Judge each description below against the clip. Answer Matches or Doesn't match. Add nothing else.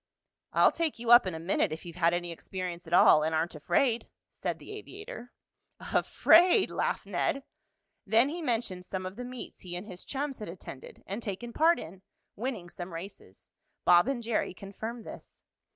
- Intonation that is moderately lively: Doesn't match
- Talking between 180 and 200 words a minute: Matches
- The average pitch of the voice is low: Doesn't match